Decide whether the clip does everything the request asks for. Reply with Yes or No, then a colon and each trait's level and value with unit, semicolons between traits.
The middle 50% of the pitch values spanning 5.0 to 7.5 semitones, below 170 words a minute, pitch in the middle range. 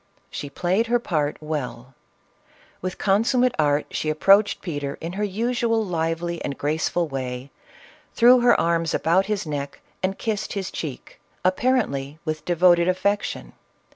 Yes: wide, 5.4 semitones; average, 140 wpm; medium, 175 Hz